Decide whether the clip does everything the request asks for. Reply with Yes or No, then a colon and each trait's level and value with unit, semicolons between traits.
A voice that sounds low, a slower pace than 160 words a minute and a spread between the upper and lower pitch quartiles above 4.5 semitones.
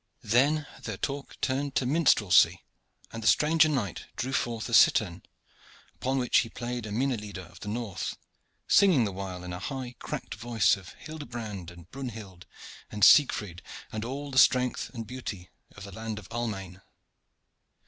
No: low, 115 Hz; average, 165 wpm; average, 4.9 semitones